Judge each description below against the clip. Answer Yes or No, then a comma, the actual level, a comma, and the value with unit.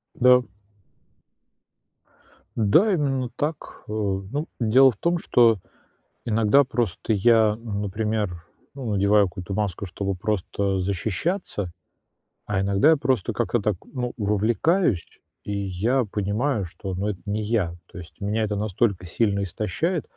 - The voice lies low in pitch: Yes, low, 105 Hz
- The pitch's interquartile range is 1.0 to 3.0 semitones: No, average, 3.8 semitones